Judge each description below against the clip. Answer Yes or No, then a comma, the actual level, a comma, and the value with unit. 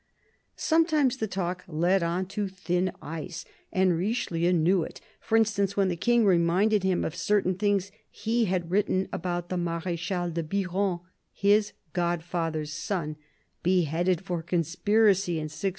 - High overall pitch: No, medium, 180 Hz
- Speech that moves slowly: No, average, 145 wpm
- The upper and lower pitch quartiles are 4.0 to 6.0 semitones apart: No, average, 2.9 semitones